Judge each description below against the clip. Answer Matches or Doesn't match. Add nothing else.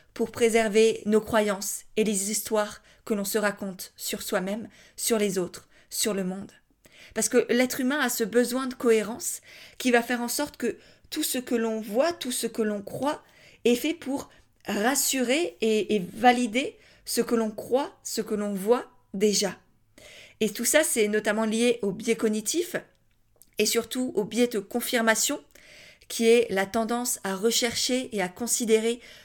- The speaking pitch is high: Matches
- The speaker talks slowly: Doesn't match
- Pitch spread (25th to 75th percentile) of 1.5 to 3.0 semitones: Matches